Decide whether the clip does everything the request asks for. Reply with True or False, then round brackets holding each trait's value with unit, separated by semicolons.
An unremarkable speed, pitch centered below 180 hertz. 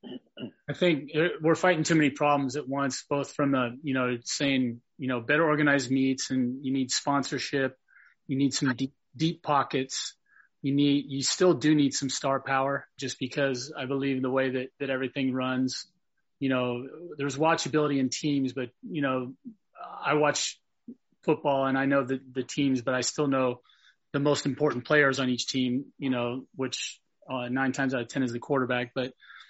True (185 wpm; 135 Hz)